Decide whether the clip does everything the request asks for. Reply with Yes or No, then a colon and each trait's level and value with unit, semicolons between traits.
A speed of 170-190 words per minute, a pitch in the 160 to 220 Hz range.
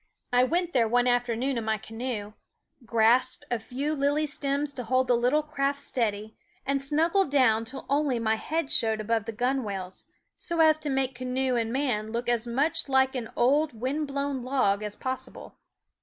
No: average, 180 wpm; very high, 255 Hz